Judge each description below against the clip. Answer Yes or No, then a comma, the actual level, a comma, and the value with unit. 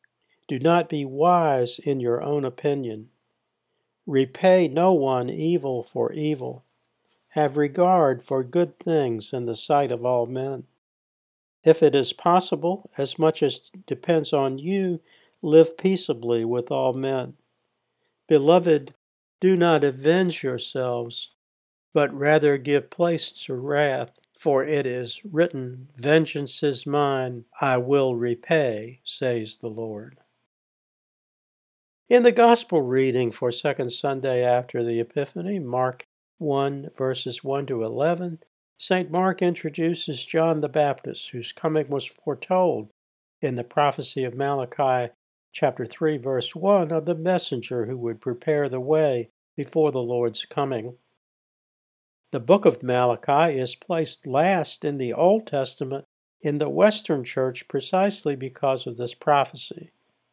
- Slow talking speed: Yes, slow, 130 wpm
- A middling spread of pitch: Yes, average, 4.4 semitones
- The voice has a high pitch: No, medium, 140 Hz